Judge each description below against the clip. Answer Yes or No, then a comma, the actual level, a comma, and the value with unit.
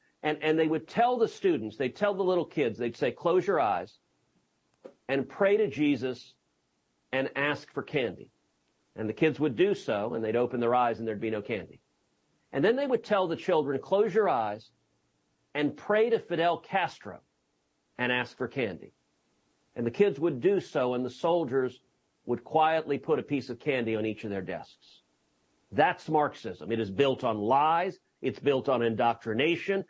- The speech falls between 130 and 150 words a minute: No, average, 185 wpm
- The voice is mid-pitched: No, low, 130 Hz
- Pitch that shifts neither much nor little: No, wide, 7.1 semitones